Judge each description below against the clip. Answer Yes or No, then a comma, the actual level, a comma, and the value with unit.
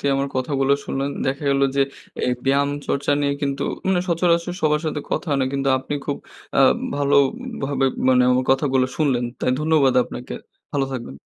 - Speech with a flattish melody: Yes, narrow, 1.8 semitones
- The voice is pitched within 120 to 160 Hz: Yes, medium, 140 Hz